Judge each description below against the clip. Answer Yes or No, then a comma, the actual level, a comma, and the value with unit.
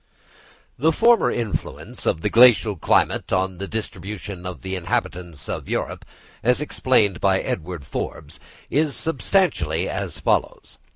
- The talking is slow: Yes, slow, 130 wpm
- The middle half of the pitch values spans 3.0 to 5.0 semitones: No, wide, 5.6 semitones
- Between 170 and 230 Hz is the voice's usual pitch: No, low, 100 Hz